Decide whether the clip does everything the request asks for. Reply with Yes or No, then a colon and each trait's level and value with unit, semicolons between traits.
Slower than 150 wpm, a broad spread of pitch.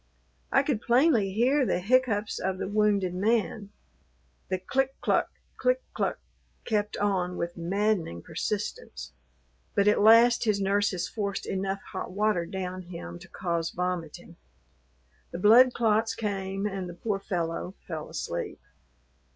No: slow, 135 wpm; average, 3.2 semitones